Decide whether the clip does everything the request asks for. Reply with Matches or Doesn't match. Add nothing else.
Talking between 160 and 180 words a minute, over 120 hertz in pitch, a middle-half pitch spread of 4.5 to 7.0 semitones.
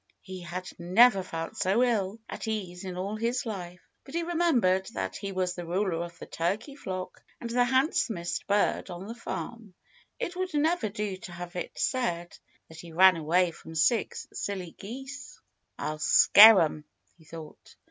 Matches